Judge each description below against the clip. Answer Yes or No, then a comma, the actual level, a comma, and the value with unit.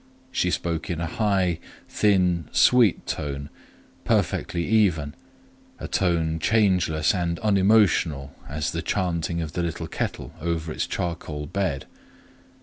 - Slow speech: Yes, slow, 120 wpm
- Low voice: Yes, very low, 85 Hz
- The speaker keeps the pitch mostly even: No, average, 3.2 semitones